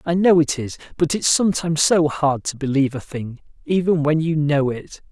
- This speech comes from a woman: No, male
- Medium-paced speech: No, fast, 210 wpm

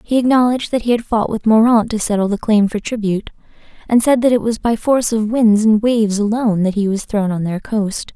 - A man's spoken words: No, female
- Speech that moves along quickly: Yes, fast, 245 wpm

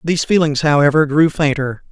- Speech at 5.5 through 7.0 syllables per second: Yes, 5.7 syllables/s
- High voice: No, medium, 150 Hz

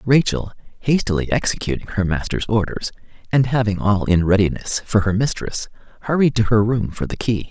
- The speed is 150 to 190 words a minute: Yes, average, 170 wpm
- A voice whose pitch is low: Yes, low, 110 Hz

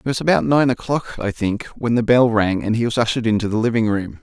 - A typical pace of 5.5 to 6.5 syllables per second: Yes, 6.1 syllables/s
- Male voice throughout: Yes, male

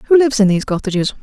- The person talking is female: Yes, female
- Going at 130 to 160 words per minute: No, fast, 245 wpm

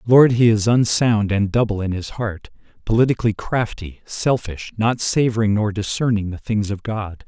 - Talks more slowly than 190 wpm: Yes, average, 165 wpm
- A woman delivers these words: No, male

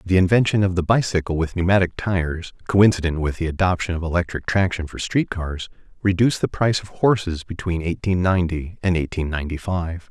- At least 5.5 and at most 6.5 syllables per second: Yes, 5.8 syllables/s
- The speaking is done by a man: Yes, male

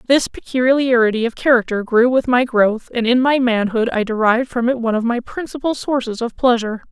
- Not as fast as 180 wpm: No, average, 200 wpm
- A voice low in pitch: No, high, 240 Hz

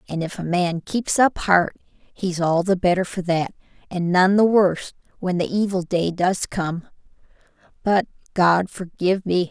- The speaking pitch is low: No, medium, 180 Hz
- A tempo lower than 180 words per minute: Yes, average, 170 wpm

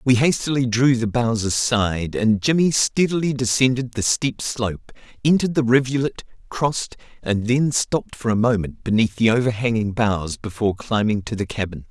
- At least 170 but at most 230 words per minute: No, average, 160 wpm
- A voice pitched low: Yes, low, 120 Hz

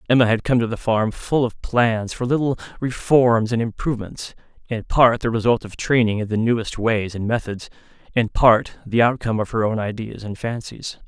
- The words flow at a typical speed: Yes, average, 195 wpm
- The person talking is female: No, male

